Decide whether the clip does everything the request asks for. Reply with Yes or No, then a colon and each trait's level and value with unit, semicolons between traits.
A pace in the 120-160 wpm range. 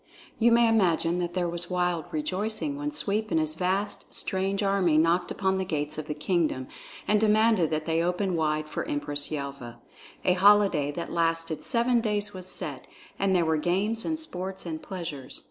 No: average, 180 wpm